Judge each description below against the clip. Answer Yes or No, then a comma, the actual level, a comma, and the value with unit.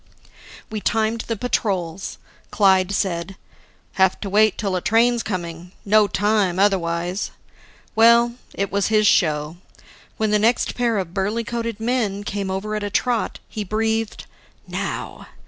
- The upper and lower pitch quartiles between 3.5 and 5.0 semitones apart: No, average, 2.8 semitones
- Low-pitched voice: No, high, 205 Hz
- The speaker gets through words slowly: No, average, 145 wpm